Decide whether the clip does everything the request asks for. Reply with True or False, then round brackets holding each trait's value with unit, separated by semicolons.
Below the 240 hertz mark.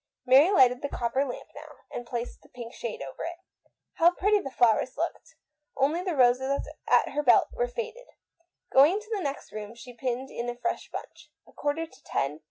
False (270 Hz)